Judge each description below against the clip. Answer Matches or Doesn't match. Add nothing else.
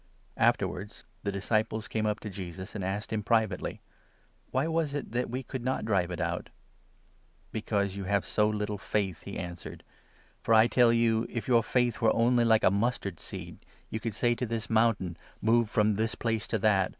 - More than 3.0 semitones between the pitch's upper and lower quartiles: Doesn't match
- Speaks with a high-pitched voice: Doesn't match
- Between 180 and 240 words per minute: Matches